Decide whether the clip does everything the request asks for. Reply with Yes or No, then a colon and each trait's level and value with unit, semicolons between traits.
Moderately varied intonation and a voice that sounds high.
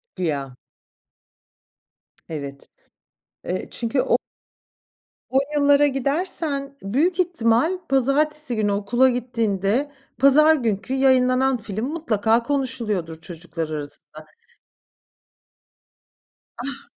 No: wide, 6.2 semitones; high, 245 Hz